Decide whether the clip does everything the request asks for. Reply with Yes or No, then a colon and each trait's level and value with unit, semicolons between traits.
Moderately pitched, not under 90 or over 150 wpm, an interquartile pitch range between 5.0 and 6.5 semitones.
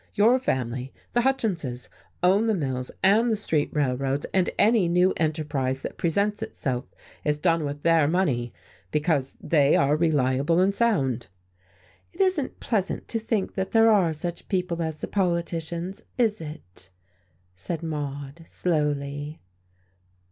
Yes: medium, 165 Hz; average, 140 wpm; average, 5.3 semitones